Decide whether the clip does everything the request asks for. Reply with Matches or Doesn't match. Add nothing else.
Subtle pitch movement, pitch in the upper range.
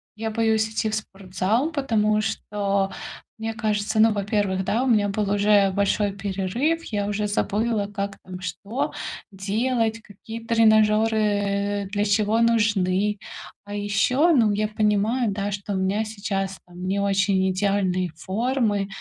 Matches